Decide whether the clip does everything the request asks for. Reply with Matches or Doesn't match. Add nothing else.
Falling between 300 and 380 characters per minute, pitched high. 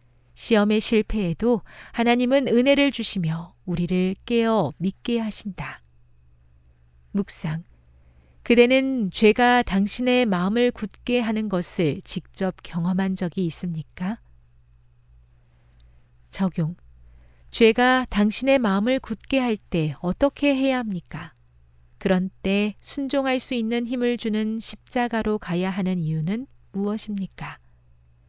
Doesn't match